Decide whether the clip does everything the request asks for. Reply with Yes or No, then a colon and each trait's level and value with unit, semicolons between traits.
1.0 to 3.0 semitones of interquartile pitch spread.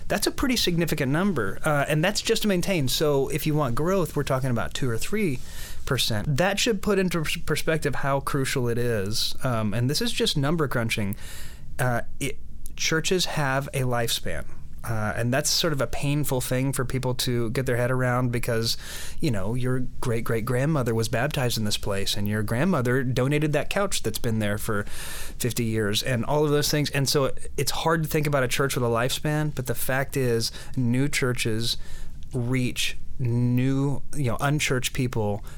No: average, 4.3 semitones